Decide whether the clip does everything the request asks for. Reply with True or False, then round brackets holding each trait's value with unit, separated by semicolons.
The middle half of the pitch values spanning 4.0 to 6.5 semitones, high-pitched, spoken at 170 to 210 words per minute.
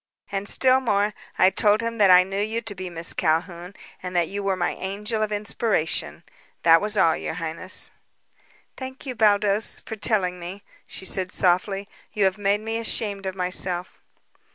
False (2.7 semitones; 195 Hz; 175 wpm)